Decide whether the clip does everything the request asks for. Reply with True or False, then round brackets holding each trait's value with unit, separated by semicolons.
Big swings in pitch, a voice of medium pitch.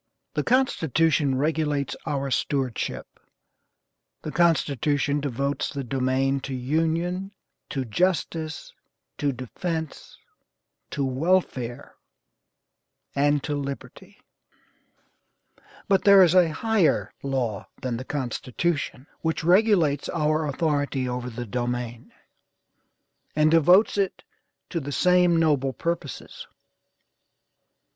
False (4.0 semitones; 145 Hz)